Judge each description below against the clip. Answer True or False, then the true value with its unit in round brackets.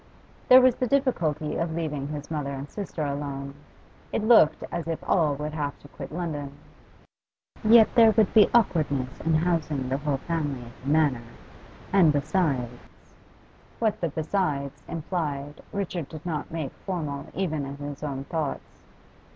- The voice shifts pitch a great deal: False (3.7 semitones)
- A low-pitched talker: False (155 Hz)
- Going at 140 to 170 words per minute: True (155 wpm)